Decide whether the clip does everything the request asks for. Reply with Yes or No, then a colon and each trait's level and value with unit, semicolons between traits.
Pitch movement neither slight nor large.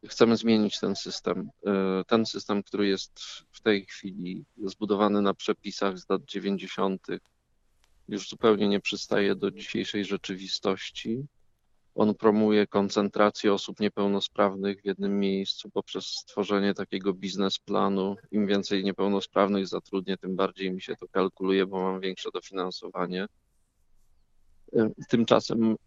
No: narrow, 1.4 semitones